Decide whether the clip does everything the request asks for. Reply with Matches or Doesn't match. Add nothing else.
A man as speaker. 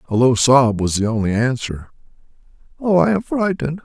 Matches